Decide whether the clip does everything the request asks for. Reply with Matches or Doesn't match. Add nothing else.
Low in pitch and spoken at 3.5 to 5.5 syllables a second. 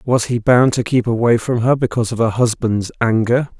Matches